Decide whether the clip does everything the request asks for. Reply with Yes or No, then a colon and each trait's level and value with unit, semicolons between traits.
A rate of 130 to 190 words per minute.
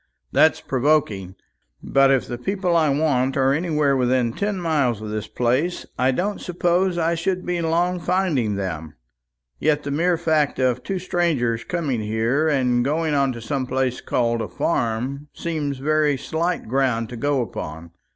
Yes: average, 165 wpm